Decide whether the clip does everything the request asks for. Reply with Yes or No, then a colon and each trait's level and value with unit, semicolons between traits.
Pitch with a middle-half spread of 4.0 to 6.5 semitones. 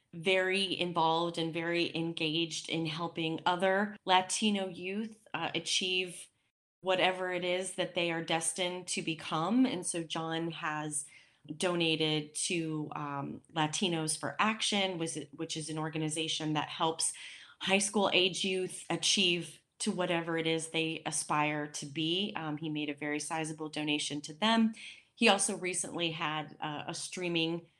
No: average, 2.8 semitones